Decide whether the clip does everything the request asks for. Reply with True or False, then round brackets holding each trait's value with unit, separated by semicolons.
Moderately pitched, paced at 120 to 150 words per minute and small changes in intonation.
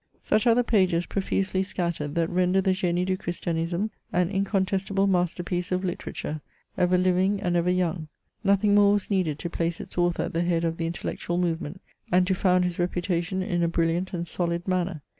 False (180 Hz; 190 wpm; 1.8 semitones)